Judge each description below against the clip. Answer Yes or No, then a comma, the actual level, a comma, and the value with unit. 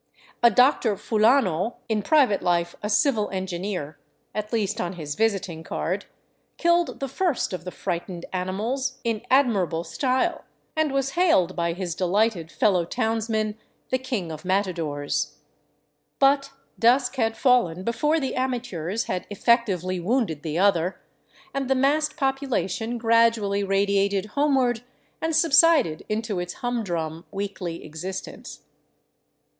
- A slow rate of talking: Yes, slow, 130 wpm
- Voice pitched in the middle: No, high, 210 Hz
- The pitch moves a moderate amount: No, wide, 6.0 semitones